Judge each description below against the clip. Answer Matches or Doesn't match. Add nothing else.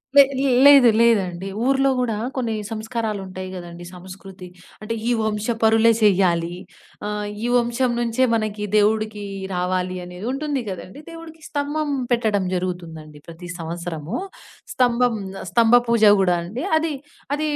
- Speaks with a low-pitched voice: Doesn't match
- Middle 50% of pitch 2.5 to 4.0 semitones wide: Doesn't match